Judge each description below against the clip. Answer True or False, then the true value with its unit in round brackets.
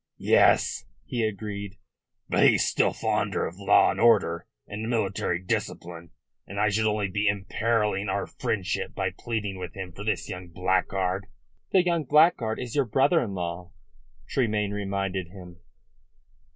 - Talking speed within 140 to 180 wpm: True (150 wpm)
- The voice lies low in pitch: True (100 Hz)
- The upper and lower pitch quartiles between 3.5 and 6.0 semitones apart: False (3.1 semitones)